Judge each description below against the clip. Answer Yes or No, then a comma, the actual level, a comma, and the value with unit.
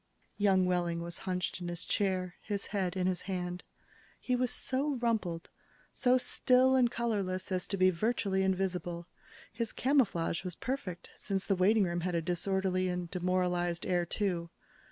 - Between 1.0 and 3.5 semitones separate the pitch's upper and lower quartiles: Yes, average, 3.0 semitones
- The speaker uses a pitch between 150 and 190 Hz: Yes, medium, 185 Hz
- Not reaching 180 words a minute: Yes, average, 160 wpm